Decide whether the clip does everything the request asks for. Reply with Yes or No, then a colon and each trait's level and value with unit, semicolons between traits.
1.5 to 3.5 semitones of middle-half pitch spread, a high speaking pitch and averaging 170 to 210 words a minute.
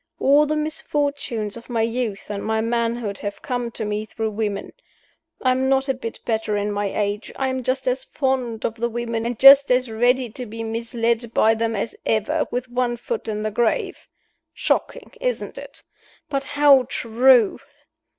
Yes: average, 2.9 semitones; high, 235 Hz; average, 180 wpm